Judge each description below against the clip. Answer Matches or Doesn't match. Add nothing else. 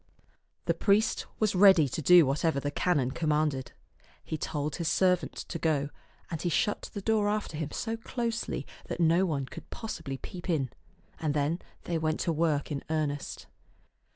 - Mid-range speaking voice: Matches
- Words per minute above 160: Matches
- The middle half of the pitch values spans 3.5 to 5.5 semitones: Matches